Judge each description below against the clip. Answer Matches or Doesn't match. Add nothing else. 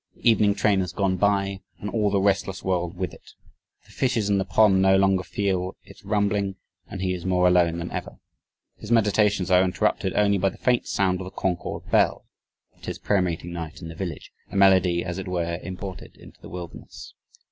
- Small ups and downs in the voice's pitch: Matches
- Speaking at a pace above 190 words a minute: Matches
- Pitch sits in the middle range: Doesn't match